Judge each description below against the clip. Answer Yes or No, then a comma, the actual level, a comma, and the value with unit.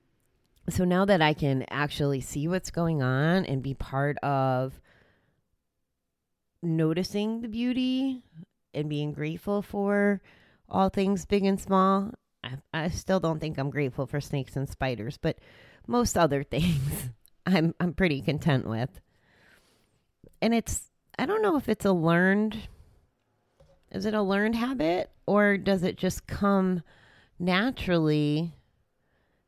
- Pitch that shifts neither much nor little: No, wide, 6.1 semitones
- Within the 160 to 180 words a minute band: No, slow, 135 wpm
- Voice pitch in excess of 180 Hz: No, medium, 165 Hz